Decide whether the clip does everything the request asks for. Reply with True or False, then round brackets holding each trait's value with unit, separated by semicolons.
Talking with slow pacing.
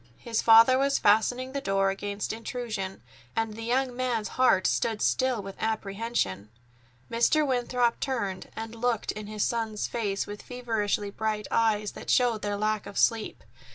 False (155 wpm)